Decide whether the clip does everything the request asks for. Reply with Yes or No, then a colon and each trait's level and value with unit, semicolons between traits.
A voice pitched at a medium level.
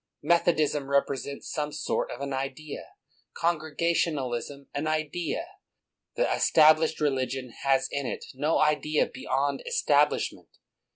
Yes: medium, 145 Hz